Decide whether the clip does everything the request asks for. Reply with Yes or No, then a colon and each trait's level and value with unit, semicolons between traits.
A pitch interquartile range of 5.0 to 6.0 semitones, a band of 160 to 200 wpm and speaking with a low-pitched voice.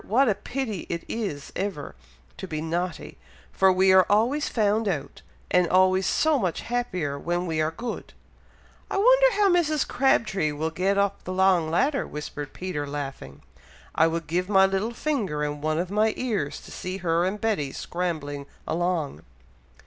No: average, 5.3 semitones; average, 170 wpm; medium, 185 Hz